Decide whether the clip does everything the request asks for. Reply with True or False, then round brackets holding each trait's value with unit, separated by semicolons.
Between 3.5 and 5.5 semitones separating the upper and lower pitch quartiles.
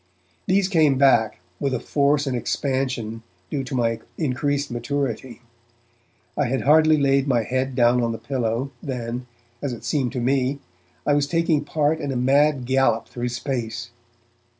False (3.0 semitones)